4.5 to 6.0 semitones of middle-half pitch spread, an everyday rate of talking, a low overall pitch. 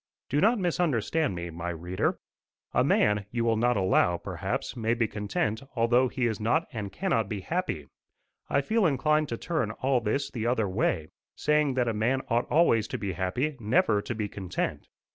Yes: average, 5.2 semitones; average, 180 wpm; low, 115 Hz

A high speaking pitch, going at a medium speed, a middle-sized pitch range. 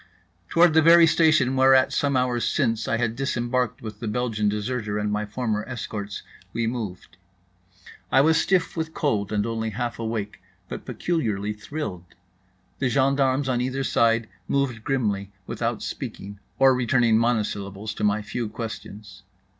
No: low, 115 Hz; average, 150 wpm; average, 3.9 semitones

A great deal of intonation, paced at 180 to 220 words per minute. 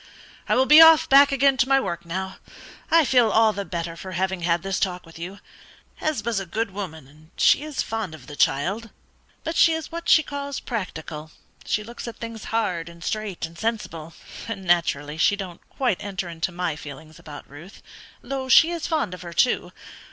Yes: wide, 6.6 semitones; average, 200 wpm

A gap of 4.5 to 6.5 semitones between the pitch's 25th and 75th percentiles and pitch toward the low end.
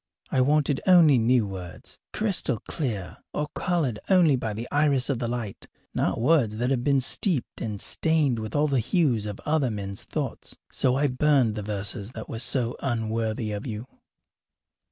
Yes: average, 5.0 semitones; low, 125 Hz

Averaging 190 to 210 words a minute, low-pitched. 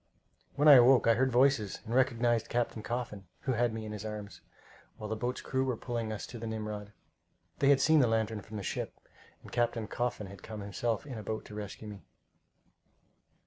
Yes: fast, 205 wpm; low, 115 Hz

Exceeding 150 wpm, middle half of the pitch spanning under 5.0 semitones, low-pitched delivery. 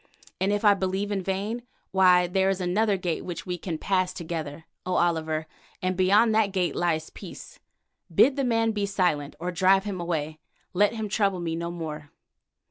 No: average, 185 wpm; average, 2.9 semitones; medium, 185 Hz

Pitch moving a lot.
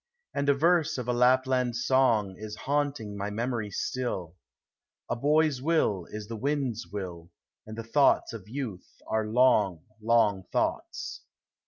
No: average, 4.3 semitones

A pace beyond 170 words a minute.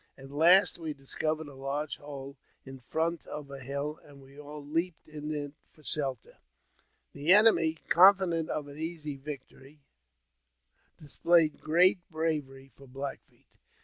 No: average, 145 wpm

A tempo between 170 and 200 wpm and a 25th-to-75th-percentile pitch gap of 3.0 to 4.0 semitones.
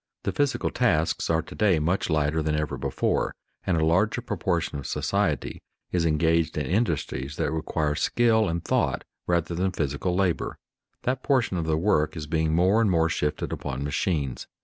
Yes: average, 175 wpm; average, 3.6 semitones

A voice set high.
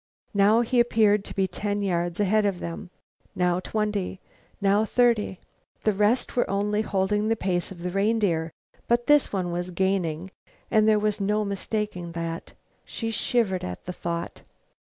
Yes: high, 200 Hz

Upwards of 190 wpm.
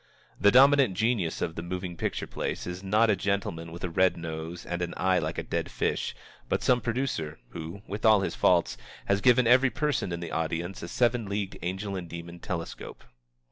Yes: average, 200 wpm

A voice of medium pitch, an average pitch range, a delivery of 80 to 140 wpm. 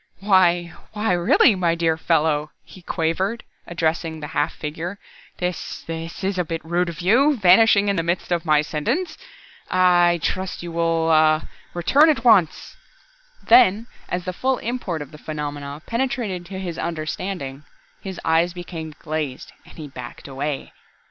No: medium, 175 Hz; average, 3.2 semitones; average, 160 wpm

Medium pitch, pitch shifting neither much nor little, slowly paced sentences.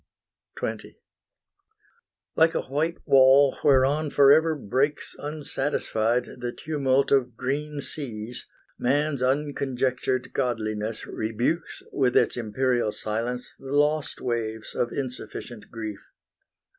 No: low, 130 Hz; average, 3.2 semitones; slow, 100 wpm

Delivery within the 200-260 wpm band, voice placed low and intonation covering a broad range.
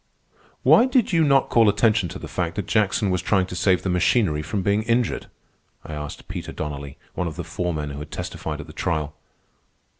Yes: fast, 205 wpm; very low, 90 Hz; wide, 5.7 semitones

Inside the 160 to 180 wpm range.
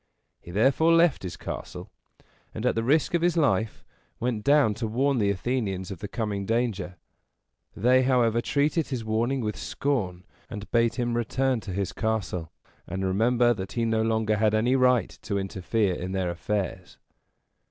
Yes: average, 170 wpm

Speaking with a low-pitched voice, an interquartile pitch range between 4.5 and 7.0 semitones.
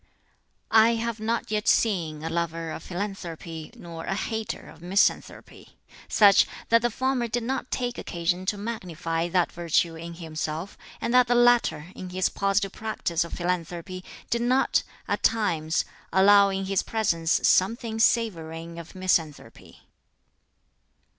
No: medium, 185 Hz; average, 4.9 semitones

